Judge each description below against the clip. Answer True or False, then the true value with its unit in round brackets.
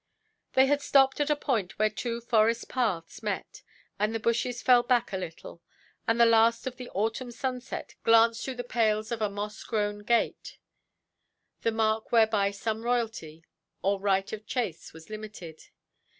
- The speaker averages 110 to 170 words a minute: True (160 wpm)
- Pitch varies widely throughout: False (2.7 semitones)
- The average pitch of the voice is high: True (225 Hz)